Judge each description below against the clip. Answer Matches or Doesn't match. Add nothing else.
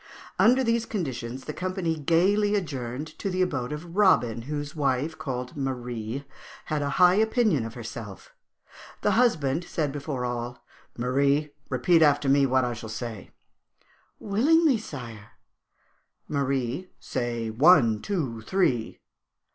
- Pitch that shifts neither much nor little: Doesn't match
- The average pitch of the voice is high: Doesn't match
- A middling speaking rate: Doesn't match